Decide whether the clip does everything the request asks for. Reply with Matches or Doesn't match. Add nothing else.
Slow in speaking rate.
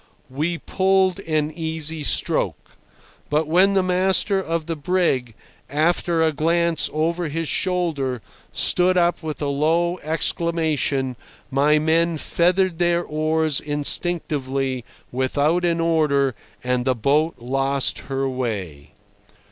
Matches